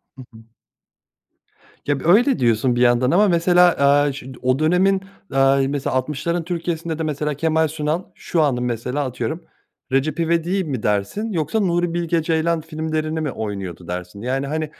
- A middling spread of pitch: Yes, average, 4.5 semitones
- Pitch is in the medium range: Yes, medium, 155 Hz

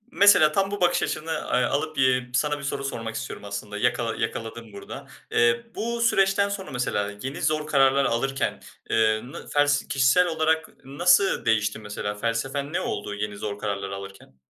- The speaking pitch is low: Yes, low, 130 Hz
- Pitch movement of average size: No, wide, 6.0 semitones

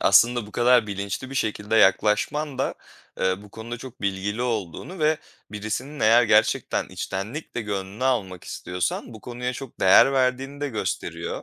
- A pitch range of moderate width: Yes, average, 4.0 semitones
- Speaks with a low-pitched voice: Yes, low, 110 Hz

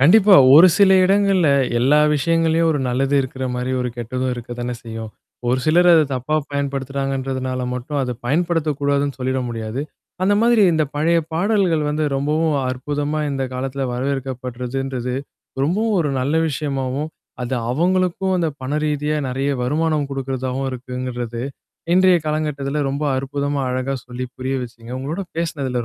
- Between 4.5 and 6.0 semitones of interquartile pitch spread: No, average, 3.6 semitones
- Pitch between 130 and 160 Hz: Yes, medium, 140 Hz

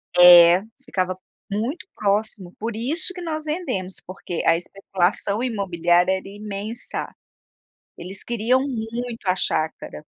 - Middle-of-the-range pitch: No, high, 200 Hz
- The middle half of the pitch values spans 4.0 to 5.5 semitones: Yes, average, 4.5 semitones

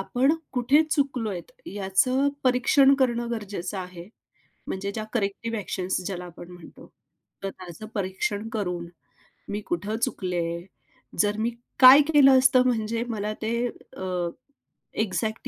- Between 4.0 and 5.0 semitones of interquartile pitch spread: Yes, average, 4.6 semitones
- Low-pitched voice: No, high, 215 Hz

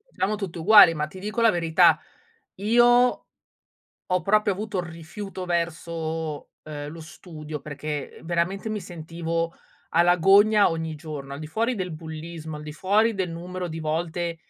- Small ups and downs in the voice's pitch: No, average, 3.7 semitones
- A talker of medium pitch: Yes, medium, 170 Hz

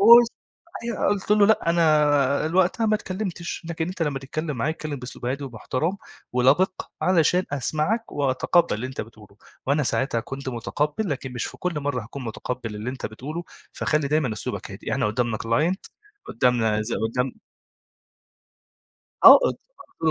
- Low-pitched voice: No, medium, 145 Hz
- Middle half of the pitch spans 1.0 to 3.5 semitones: No, wide, 5.4 semitones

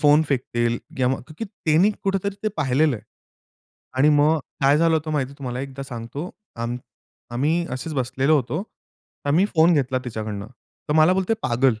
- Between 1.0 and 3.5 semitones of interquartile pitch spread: No, average, 4.1 semitones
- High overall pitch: No, medium, 140 Hz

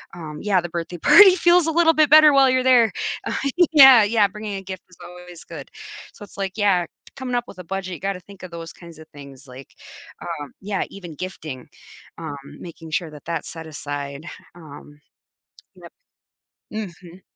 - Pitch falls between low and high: Yes, medium, 180 Hz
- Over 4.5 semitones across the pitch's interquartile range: Yes, average, 5.0 semitones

